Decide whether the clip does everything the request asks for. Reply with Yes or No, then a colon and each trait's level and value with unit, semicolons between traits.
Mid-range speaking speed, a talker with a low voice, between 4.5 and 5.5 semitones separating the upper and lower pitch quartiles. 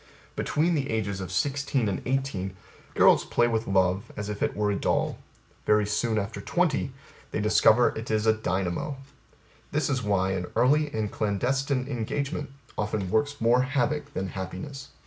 Yes: average, 165 wpm; low, 110 Hz; average, 5.2 semitones